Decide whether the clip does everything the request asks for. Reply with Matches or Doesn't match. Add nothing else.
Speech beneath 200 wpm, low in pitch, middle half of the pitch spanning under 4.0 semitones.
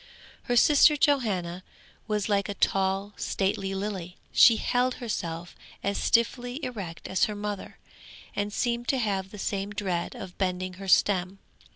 Doesn't match